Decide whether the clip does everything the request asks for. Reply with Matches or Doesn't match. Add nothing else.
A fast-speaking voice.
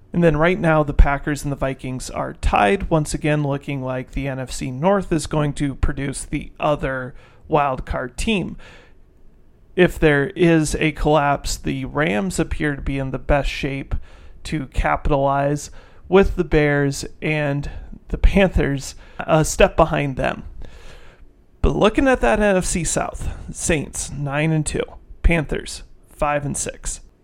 Doesn't match